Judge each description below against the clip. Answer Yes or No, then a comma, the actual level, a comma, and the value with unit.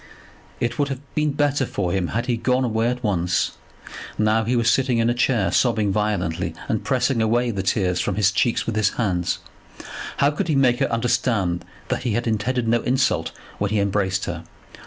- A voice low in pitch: Yes, low, 115 Hz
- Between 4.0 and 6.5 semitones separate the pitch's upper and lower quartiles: No, average, 3.6 semitones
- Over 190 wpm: Yes, average, 200 wpm